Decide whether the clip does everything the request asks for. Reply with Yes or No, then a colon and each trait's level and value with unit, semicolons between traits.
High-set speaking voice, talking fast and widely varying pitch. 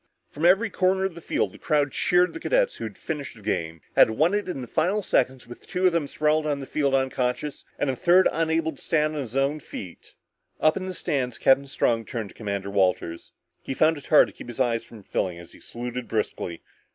No: medium, 140 Hz; fast, 235 wpm; wide, 5.7 semitones